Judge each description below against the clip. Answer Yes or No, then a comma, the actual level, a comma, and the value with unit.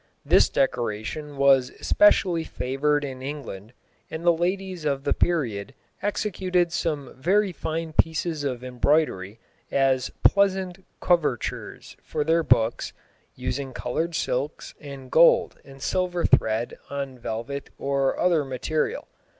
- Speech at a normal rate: No, slow, 120 wpm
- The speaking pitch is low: No, medium, 145 Hz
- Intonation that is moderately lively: Yes, average, 4.6 semitones